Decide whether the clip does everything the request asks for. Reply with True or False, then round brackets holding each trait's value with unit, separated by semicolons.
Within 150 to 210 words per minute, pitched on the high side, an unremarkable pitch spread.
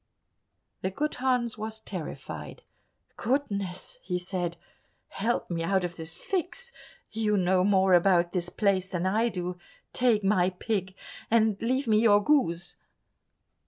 False (135 wpm; 195 Hz; 3.9 semitones)